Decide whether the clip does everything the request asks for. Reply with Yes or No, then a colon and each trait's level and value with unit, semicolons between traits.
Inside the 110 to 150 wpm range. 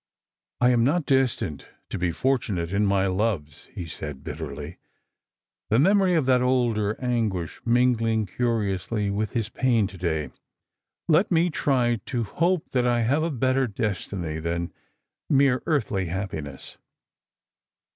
Yes: average, 145 wpm